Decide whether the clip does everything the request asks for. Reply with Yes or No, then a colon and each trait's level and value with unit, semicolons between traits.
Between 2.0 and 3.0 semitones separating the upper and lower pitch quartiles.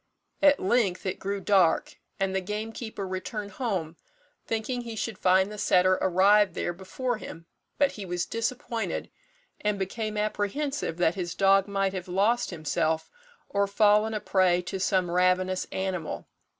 Yes: narrow, 2.6 semitones